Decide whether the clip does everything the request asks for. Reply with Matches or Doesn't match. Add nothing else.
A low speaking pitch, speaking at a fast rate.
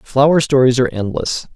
Doesn't match